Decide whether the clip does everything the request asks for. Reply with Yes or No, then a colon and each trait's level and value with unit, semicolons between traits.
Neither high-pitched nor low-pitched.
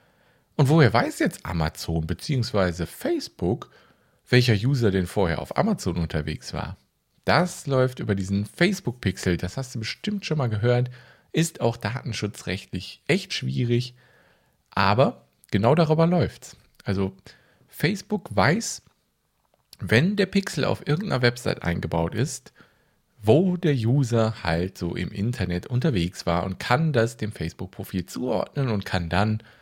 No: low, 110 Hz